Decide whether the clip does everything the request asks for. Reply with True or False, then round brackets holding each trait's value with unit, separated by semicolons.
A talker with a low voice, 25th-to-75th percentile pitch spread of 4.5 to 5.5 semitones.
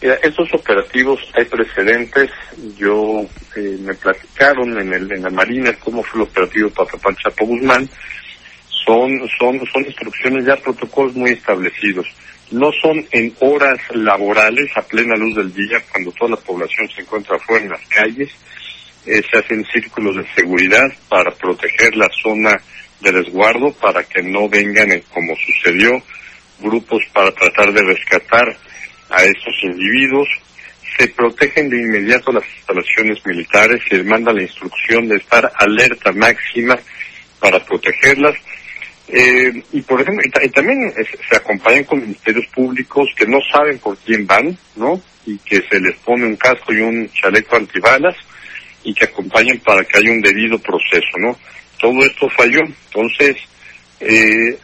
False (115 Hz; 3.6 semitones)